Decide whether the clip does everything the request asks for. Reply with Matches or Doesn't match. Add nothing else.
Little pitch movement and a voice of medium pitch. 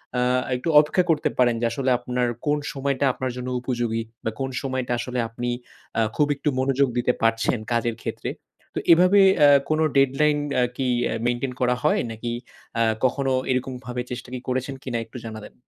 Doesn't match